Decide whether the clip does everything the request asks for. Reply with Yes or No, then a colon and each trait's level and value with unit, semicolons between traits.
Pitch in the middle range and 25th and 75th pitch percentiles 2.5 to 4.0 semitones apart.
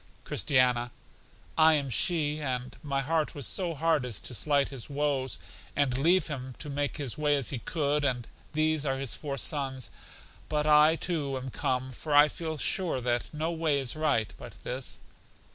Yes: medium, 145 Hz; average, 2.8 semitones